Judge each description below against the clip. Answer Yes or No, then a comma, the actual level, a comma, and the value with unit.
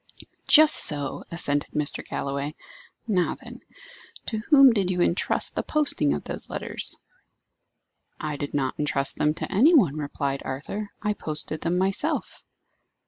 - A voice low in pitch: No, medium, 160 Hz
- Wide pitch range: Yes, wide, 6.6 semitones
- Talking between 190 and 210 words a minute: No, average, 140 wpm